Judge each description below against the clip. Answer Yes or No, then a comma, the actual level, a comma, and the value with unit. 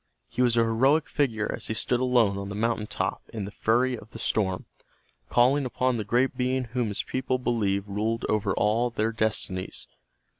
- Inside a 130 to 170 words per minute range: No, average, 190 wpm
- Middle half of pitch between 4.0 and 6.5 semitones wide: No, average, 3.0 semitones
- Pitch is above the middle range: No, low, 115 Hz